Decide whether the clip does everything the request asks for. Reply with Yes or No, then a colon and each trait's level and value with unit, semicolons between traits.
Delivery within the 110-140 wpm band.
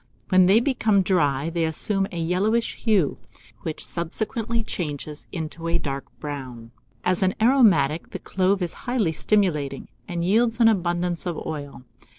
No: average, 150 wpm